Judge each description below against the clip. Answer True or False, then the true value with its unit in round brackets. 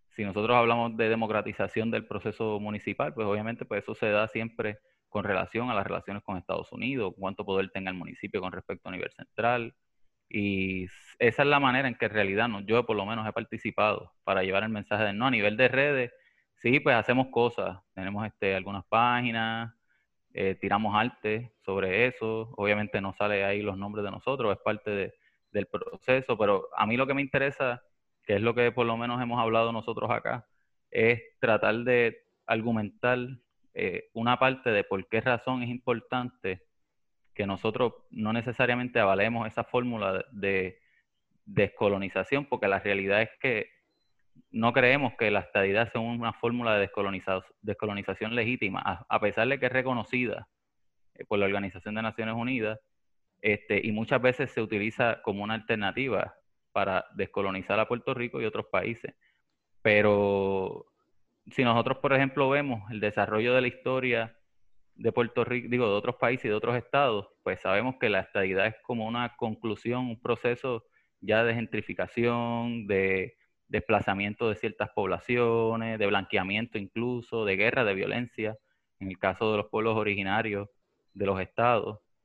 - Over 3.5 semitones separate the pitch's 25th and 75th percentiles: False (3.0 semitones)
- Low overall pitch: True (110 Hz)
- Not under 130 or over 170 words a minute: True (165 wpm)